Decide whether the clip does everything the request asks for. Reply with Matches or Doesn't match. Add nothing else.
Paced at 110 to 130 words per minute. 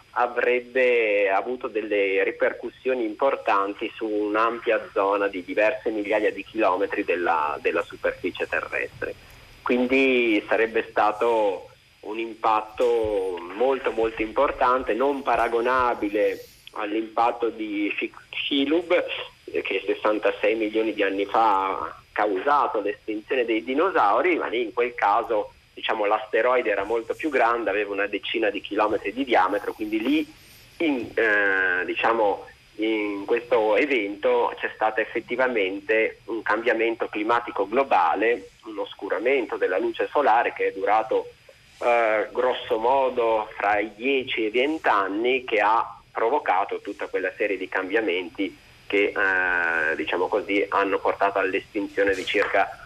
Matches